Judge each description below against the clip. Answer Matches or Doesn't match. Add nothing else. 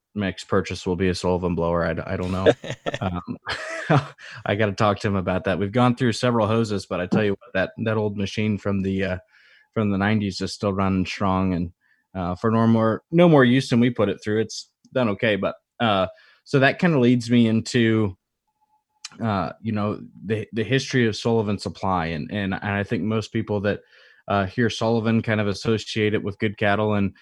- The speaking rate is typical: Doesn't match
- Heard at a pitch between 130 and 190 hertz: Doesn't match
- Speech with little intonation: Doesn't match